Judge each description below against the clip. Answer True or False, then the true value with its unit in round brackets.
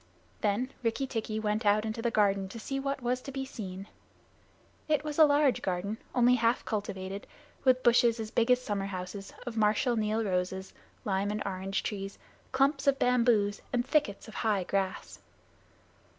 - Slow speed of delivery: False (170 wpm)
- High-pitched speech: True (220 Hz)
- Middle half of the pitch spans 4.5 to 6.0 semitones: False (3.9 semitones)